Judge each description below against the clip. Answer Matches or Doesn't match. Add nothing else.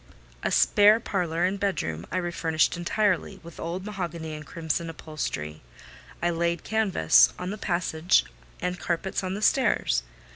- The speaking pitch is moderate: Matches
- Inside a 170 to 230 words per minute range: Doesn't match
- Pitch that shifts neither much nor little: Matches